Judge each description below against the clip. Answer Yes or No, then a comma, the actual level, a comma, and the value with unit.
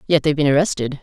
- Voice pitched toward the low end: No, medium, 145 Hz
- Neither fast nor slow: No, fast, 235 wpm